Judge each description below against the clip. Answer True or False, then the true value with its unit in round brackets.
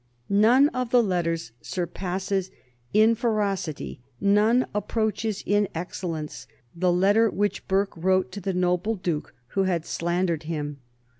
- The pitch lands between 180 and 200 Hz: True (190 Hz)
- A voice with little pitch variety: False (3.2 semitones)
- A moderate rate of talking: False (130 wpm)